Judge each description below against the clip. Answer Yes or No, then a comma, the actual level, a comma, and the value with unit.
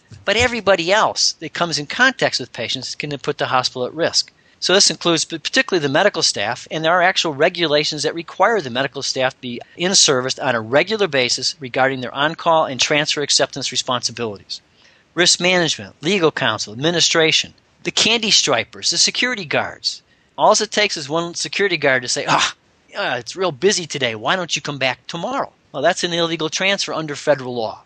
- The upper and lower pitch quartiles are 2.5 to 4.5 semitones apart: No, average, 5.2 semitones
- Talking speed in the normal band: Yes, average, 185 wpm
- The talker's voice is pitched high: No, medium, 155 Hz